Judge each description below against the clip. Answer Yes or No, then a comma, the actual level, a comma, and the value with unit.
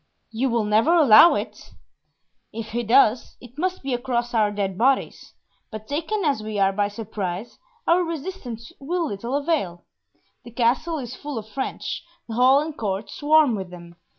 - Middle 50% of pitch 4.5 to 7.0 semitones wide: Yes, average, 5.3 semitones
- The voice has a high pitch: Yes, high, 240 Hz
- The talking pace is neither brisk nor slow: Yes, average, 170 wpm